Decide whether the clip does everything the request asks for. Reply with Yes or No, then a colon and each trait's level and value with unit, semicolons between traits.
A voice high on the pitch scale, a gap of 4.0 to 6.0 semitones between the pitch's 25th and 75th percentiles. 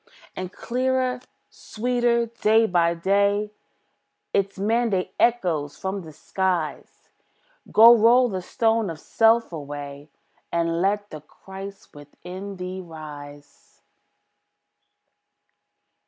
Yes: high, 195 Hz; average, 5.2 semitones